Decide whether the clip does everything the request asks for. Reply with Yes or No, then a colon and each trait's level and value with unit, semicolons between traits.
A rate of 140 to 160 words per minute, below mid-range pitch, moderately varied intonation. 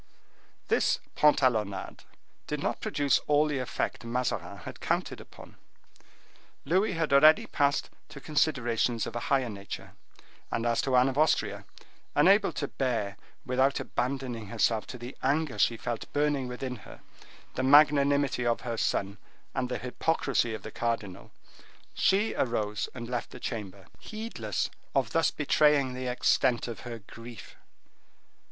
Yes: average, 145 wpm; low, 125 Hz; average, 3.6 semitones